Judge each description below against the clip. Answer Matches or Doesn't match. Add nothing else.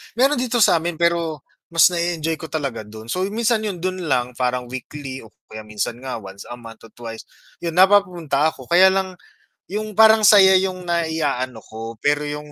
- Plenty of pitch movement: Matches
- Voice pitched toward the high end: Doesn't match